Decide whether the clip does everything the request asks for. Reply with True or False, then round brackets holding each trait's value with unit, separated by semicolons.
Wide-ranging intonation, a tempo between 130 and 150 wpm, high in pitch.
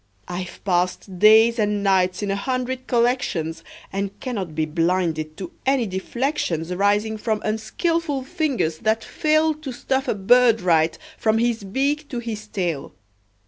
True (5.7 semitones; 145 wpm; 215 Hz)